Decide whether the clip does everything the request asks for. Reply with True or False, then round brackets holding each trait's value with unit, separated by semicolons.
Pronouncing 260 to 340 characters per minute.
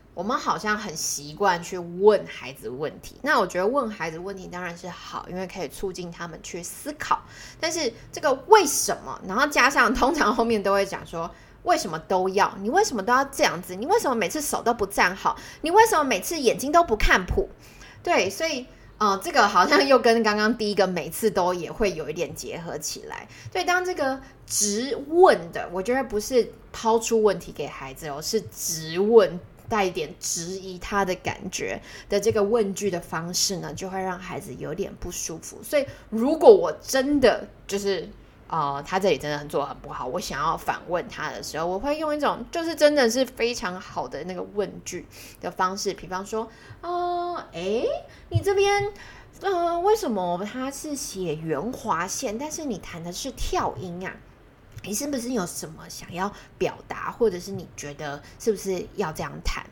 True (275 characters per minute)